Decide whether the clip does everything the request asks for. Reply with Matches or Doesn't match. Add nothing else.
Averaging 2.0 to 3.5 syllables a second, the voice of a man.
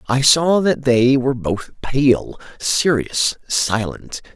Matches